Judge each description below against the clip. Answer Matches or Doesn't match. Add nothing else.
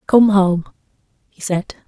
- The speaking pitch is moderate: Doesn't match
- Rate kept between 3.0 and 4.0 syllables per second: Matches